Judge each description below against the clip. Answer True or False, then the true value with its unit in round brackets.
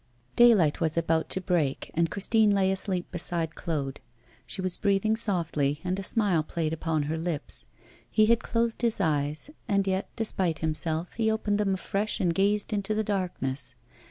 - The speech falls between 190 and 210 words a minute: False (170 wpm)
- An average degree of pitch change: True (4.5 semitones)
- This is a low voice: False (185 Hz)